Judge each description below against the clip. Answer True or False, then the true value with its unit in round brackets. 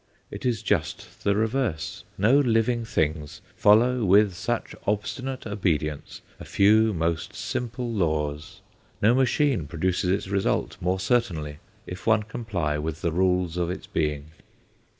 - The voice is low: True (95 Hz)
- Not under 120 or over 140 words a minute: True (135 wpm)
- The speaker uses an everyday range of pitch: False (5.7 semitones)